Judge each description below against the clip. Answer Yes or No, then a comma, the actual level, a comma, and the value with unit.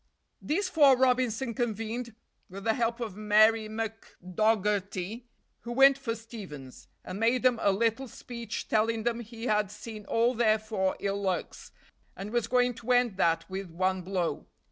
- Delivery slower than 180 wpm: Yes, average, 160 wpm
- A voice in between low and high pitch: No, high, 225 Hz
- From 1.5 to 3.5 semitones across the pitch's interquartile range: Yes, average, 3.1 semitones